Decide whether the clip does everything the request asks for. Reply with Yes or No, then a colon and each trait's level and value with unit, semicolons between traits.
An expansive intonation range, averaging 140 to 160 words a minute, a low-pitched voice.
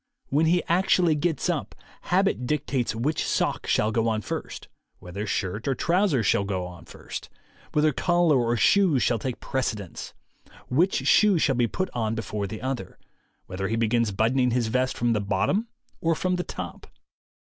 No: wide, 7.0 semitones; average, 170 wpm; low, 125 Hz